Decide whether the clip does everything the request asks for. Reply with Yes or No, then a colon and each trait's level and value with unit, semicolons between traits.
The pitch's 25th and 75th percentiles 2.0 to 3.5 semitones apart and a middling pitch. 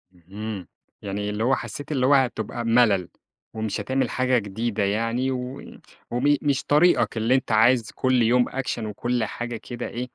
No: average, 3.0 semitones; low, 120 Hz